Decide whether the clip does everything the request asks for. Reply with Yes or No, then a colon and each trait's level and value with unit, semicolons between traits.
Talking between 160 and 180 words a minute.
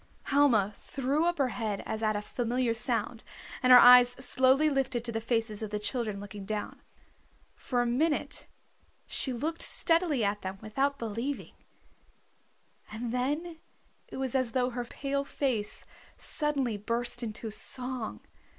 No: average, 150 wpm